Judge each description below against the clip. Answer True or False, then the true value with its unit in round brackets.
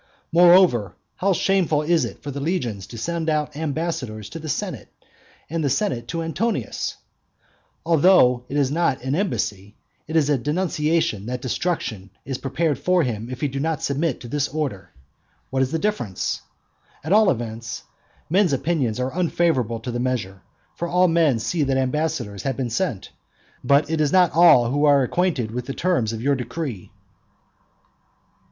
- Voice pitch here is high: False (145 Hz)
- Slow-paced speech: False (170 wpm)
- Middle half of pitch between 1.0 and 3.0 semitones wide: False (5.3 semitones)